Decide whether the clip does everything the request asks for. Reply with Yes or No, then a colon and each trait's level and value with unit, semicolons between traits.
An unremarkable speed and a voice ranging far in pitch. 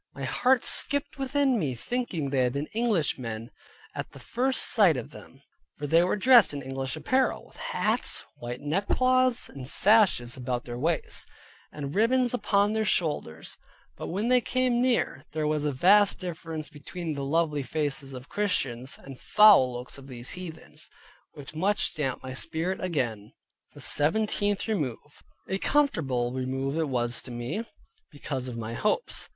Yes: average, 160 wpm; wide, 8.1 semitones